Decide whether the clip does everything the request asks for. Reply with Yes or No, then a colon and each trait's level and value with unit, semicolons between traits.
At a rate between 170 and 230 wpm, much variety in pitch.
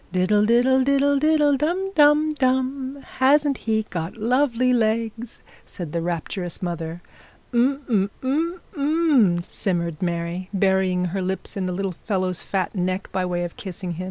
No: average, 155 wpm; wide, 7.0 semitones